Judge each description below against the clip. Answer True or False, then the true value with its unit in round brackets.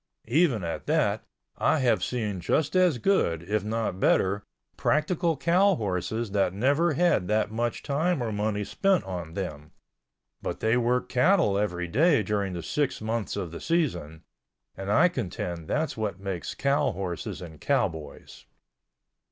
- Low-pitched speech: True (110 Hz)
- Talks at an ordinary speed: True (145 wpm)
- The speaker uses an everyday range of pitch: False (7.8 semitones)